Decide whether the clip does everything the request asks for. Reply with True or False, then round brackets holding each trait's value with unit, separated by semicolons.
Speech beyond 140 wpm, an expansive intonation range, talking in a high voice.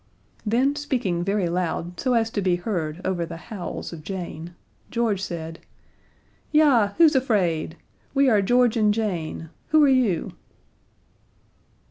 False (135 wpm; 6.0 semitones; 200 Hz)